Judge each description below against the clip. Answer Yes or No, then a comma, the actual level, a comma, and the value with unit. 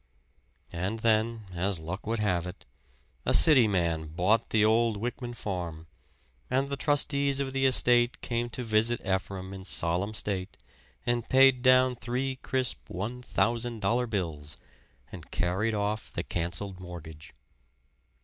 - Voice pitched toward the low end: Yes, low, 110 Hz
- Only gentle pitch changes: No, average, 4.9 semitones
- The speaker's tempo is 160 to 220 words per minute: No, average, 140 wpm